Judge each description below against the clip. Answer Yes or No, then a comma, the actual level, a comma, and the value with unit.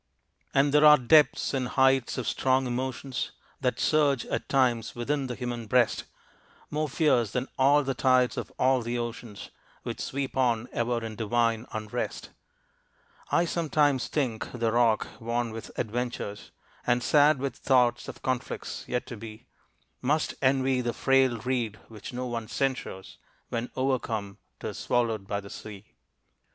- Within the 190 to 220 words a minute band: No, average, 150 wpm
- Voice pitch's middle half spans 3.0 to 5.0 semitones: No, narrow, 2.5 semitones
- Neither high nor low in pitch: No, low, 125 Hz